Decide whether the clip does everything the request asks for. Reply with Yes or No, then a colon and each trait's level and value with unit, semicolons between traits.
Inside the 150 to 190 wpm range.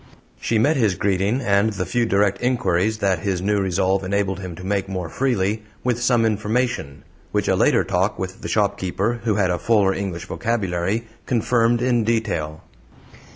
Yes: average, 170 wpm